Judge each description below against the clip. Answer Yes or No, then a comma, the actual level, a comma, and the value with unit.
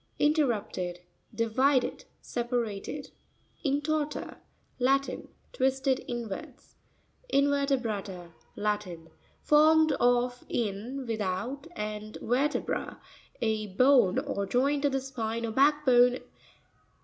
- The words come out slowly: Yes, slow, 80 wpm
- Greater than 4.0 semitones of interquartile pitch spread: Yes, average, 4.6 semitones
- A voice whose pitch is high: Yes, high, 245 Hz